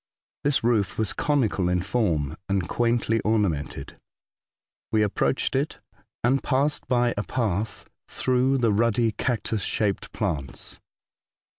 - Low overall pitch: Yes, low, 110 Hz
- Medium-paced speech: No, slow, 125 wpm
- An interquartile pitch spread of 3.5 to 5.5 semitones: Yes, average, 3.8 semitones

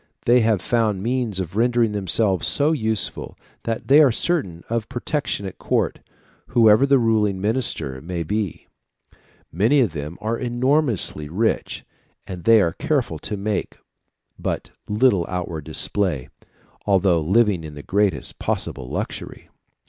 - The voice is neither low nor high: No, low, 105 Hz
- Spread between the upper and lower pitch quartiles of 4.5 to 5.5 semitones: Yes, average, 4.9 semitones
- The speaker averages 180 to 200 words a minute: No, average, 140 wpm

